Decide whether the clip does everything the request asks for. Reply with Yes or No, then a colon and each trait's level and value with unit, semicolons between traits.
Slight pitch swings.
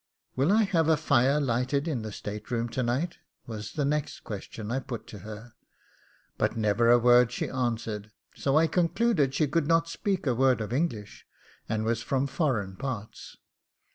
No: average, 5.0 semitones